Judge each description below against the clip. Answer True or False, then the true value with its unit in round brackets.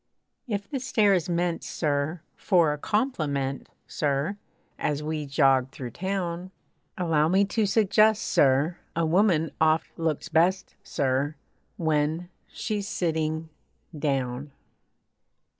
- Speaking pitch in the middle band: True (160 Hz)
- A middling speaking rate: False (115 wpm)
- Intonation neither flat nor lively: True (4.4 semitones)